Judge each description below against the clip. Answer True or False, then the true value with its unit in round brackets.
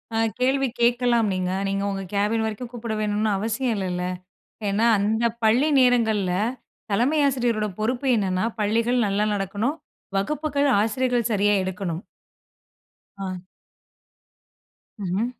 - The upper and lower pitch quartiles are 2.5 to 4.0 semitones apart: True (3.7 semitones)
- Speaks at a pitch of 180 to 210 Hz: False (220 Hz)